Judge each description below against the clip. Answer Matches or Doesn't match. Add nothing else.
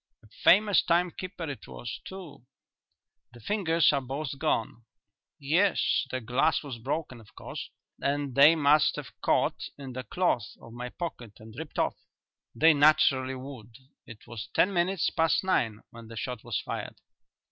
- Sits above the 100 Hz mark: Matches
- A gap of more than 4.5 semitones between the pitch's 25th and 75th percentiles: Matches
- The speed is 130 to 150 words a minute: Doesn't match